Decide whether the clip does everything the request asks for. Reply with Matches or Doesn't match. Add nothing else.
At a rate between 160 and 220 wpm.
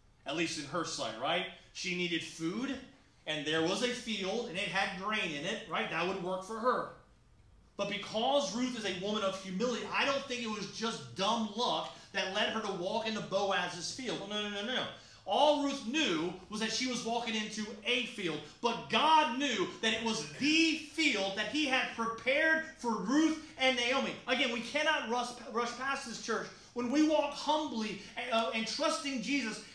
Matches